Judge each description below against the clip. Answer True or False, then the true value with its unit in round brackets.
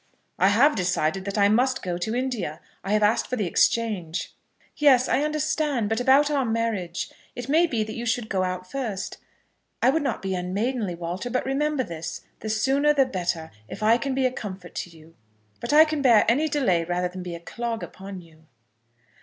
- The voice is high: True (220 Hz)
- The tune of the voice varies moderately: False (6.3 semitones)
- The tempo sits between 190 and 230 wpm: True (205 wpm)